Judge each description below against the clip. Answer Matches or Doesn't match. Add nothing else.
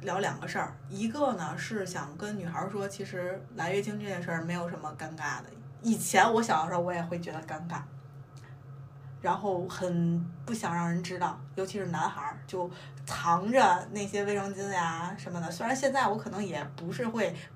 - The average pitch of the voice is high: Doesn't match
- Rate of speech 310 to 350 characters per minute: Doesn't match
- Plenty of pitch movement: Doesn't match